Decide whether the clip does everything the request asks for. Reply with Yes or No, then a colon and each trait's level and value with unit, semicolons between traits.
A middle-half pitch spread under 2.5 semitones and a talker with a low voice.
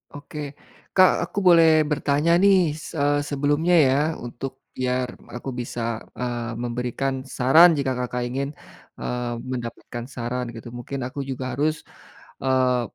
No: average, 2.9 semitones; low, 130 Hz